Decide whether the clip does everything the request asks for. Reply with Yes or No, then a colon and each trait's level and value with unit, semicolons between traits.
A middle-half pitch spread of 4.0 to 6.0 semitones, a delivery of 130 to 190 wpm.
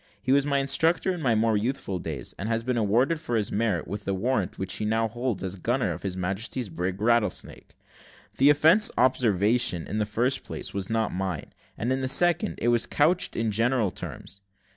No: average, 4.9 semitones; fast, 205 wpm